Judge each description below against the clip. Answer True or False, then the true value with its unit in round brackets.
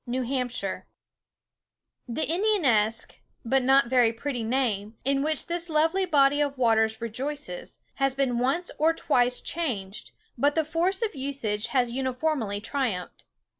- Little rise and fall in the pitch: False (4.8 semitones)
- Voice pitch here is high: True (270 Hz)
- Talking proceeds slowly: True (130 wpm)